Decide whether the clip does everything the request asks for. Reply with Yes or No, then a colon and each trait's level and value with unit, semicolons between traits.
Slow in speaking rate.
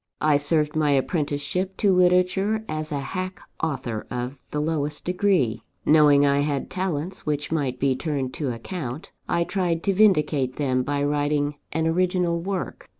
No: average, 155 wpm